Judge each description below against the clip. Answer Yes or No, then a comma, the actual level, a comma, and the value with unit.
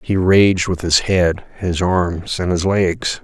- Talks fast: No, average, 185 wpm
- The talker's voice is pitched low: Yes, very low, 90 Hz